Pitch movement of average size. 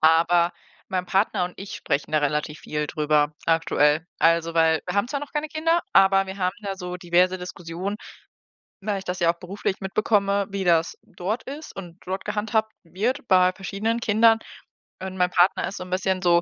Yes: average, 3.1 semitones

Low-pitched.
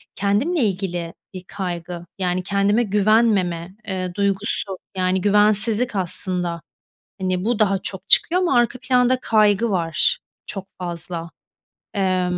No: high, 195 Hz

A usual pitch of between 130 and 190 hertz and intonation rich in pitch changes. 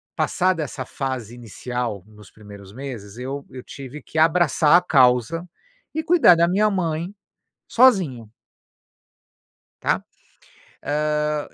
Yes: medium, 140 Hz; wide, 5.7 semitones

